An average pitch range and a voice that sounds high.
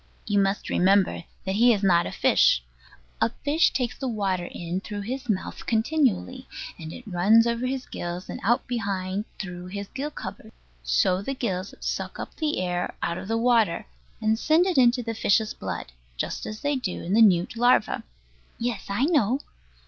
Yes: average, 4.9 semitones; high, 215 Hz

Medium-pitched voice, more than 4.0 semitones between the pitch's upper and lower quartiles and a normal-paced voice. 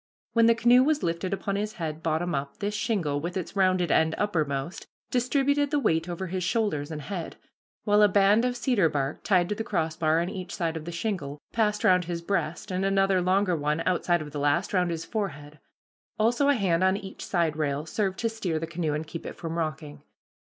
No: medium, 180 Hz; average, 4.4 semitones; fast, 215 wpm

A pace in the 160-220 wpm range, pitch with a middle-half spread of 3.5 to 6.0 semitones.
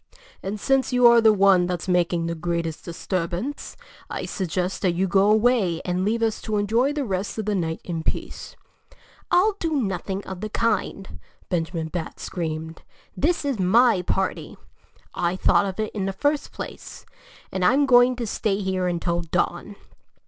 Yes: average, 170 wpm; average, 4.5 semitones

